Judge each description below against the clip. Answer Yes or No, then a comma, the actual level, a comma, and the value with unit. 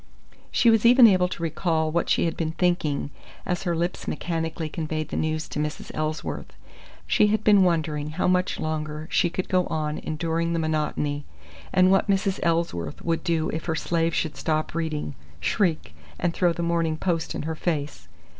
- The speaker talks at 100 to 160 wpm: No, average, 185 wpm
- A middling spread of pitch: No, narrow, 2.2 semitones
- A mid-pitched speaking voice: Yes, medium, 165 Hz